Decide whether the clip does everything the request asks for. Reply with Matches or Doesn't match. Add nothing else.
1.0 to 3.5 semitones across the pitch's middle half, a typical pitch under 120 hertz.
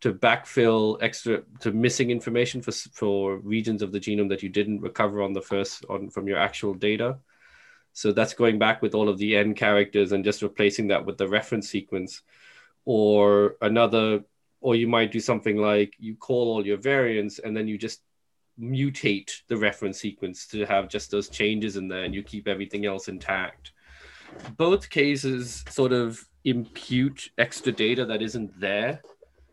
Matches